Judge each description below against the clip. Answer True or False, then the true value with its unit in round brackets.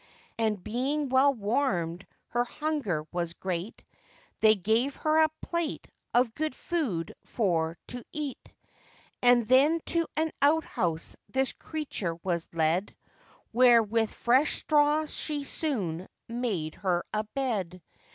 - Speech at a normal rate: False (125 wpm)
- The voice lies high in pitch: True (235 Hz)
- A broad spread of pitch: True (7.9 semitones)